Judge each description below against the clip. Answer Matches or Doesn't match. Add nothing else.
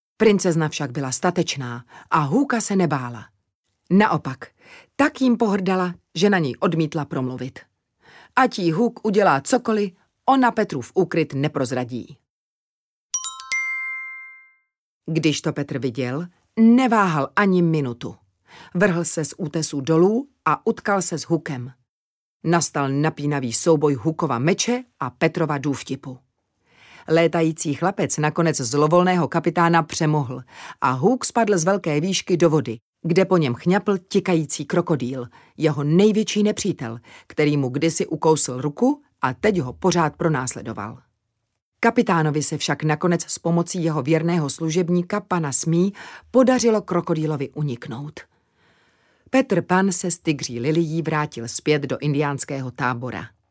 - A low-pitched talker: Doesn't match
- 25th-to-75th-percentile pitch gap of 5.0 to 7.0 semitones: Matches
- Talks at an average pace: Matches